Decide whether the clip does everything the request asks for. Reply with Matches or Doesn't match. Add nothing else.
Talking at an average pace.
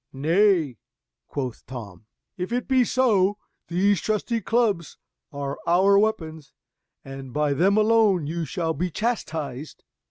Doesn't match